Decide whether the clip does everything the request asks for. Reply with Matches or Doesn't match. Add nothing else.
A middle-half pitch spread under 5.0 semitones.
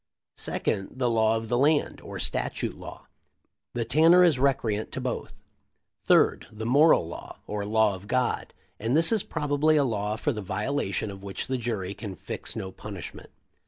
Doesn't match